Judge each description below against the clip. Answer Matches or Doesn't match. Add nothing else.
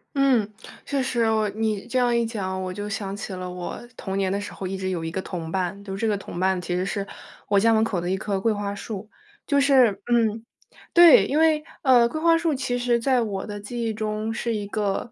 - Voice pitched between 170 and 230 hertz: Matches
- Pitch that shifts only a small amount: Doesn't match